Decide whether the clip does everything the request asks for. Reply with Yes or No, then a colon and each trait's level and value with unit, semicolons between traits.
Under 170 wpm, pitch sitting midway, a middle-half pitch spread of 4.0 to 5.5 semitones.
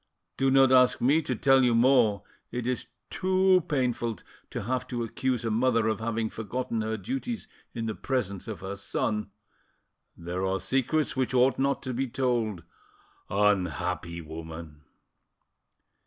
No: average, 145 wpm; low, 115 Hz; average, 4.5 semitones